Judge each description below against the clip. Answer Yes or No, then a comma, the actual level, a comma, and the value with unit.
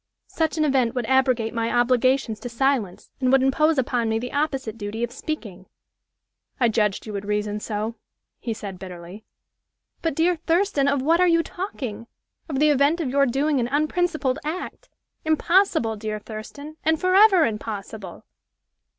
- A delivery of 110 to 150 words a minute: No, average, 160 wpm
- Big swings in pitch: Yes, wide, 5.8 semitones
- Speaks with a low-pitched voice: No, very high, 260 Hz